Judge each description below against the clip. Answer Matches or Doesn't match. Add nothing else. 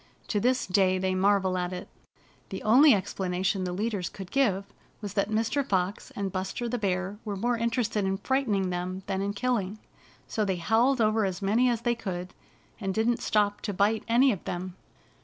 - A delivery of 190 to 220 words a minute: Matches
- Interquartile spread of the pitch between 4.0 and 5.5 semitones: Doesn't match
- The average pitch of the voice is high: Matches